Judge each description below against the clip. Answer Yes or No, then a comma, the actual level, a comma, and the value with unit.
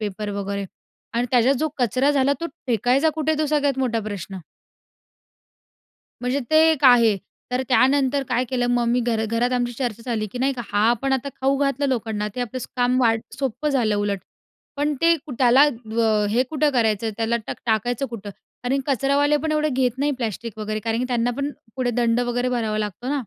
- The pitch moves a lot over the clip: No, average, 3.3 semitones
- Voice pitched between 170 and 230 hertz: No, high, 245 Hz